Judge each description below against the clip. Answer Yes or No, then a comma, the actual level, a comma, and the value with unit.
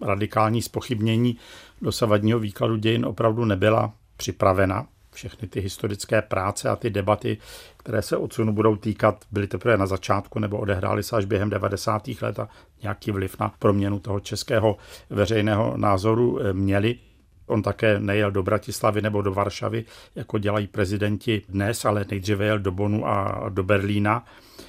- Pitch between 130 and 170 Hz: No, low, 105 Hz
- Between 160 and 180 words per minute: No, average, 150 wpm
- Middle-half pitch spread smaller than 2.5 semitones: Yes, narrow, 1.7 semitones